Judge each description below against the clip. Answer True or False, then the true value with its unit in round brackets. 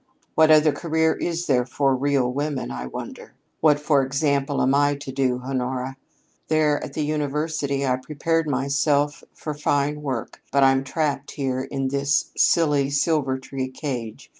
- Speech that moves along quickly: False (155 wpm)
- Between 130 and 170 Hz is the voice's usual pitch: True (140 Hz)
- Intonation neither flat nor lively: False (2.0 semitones)